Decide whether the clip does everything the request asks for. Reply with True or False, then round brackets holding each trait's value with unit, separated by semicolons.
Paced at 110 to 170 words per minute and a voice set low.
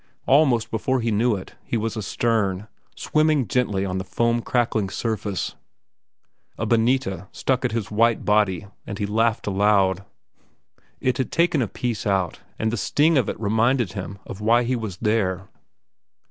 True (160 wpm; 110 Hz)